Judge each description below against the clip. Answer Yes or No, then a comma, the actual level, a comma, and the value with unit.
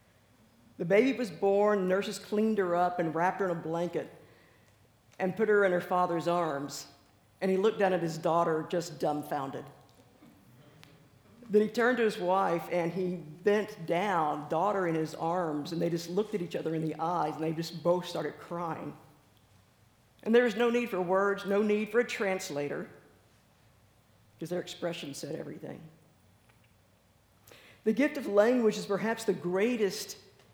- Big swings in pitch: Yes, wide, 5.8 semitones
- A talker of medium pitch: Yes, medium, 170 Hz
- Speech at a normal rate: Yes, average, 165 wpm